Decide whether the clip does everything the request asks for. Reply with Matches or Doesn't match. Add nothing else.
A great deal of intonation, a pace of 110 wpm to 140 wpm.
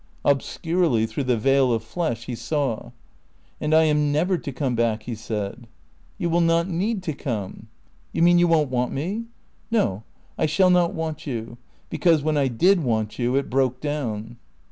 Doesn't match